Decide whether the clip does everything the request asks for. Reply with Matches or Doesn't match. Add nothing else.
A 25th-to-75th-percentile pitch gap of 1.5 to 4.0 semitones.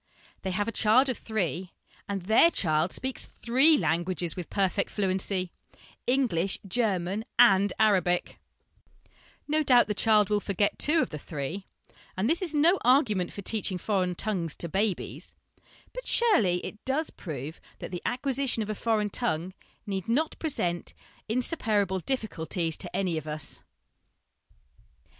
Doesn't match